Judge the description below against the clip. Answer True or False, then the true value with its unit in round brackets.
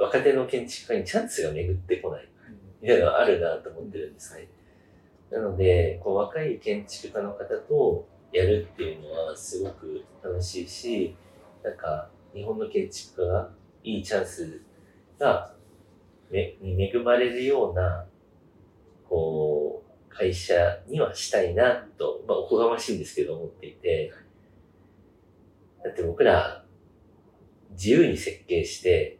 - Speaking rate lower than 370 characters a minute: True (275 characters per minute)